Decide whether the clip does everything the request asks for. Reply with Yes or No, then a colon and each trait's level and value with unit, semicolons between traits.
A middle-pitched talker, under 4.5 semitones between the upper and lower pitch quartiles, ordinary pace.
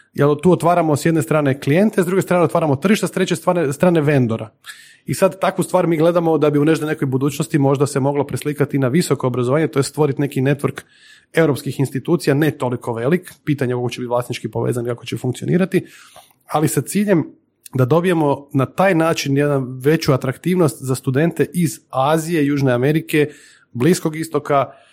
No: medium, 150 Hz; average, 3.7 semitones; fast, 180 wpm